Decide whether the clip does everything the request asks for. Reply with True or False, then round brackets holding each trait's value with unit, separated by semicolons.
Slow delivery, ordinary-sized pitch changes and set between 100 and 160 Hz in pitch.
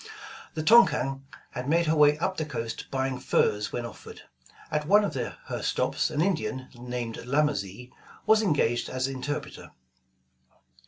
False (145 wpm; 4.0 semitones; 135 Hz)